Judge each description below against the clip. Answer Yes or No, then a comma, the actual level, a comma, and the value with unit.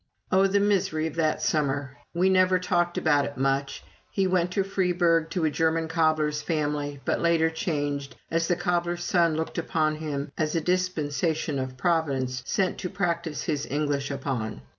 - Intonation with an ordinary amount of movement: Yes, average, 3.2 semitones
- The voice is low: No, medium, 160 Hz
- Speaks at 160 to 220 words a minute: Yes, average, 170 wpm